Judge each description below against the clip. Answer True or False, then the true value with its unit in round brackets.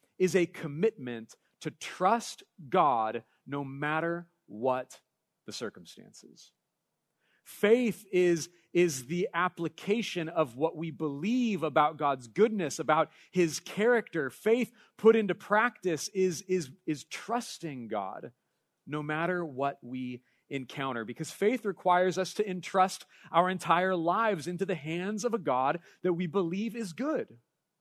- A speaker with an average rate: False (130 wpm)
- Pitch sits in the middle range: True (175 Hz)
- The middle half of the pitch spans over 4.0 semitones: True (4.6 semitones)